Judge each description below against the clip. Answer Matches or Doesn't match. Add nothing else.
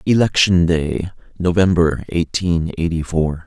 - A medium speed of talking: Doesn't match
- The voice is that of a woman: Doesn't match